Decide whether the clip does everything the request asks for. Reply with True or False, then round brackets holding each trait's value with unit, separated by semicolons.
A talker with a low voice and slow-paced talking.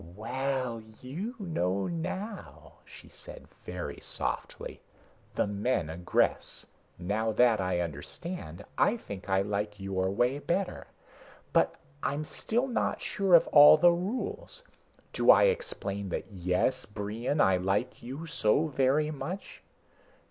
True (125 Hz; 125 wpm)